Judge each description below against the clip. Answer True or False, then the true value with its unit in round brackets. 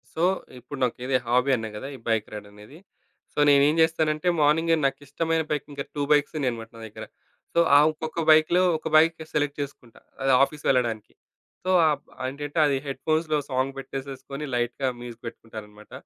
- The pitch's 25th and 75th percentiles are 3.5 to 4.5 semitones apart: True (4.1 semitones)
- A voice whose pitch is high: False (140 Hz)